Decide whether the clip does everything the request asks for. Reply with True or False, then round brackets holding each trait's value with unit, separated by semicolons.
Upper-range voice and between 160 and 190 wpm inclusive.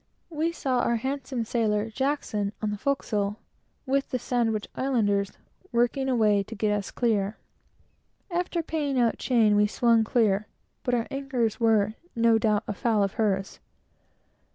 False (230 Hz; 145 wpm)